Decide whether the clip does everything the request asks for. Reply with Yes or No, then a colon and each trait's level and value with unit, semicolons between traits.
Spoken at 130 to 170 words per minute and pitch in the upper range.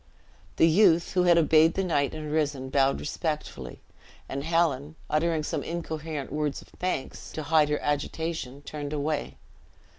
No: average, 150 wpm; medium, 155 Hz